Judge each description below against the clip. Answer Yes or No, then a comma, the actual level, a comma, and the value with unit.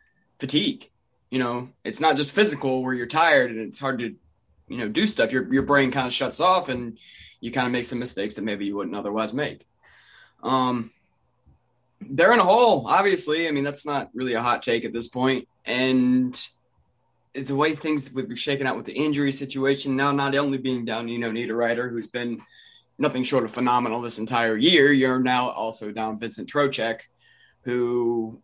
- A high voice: No, low, 125 Hz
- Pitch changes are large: No, average, 2.7 semitones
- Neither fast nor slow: Yes, average, 195 wpm